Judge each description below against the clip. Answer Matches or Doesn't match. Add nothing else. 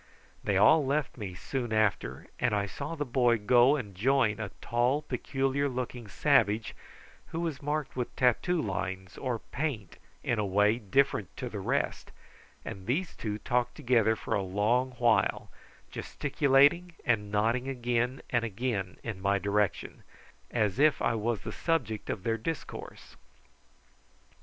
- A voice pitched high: Doesn't match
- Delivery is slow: Doesn't match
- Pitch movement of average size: Matches